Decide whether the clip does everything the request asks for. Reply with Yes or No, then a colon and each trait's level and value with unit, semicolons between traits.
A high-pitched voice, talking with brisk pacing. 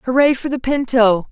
No: very high, 250 Hz; average, 185 wpm